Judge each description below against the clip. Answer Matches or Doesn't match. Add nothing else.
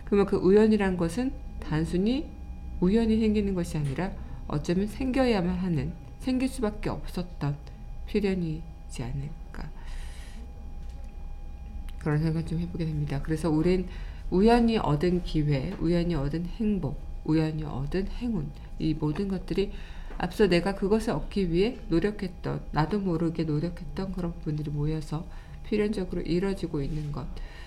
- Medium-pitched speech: Matches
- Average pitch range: Matches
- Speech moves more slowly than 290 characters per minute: Doesn't match